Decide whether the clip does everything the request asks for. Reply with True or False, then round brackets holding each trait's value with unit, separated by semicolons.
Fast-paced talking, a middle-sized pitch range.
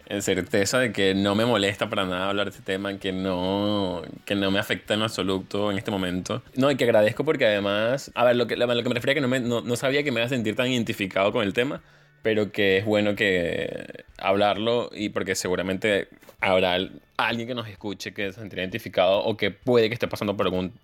True (230 wpm; 3.4 semitones)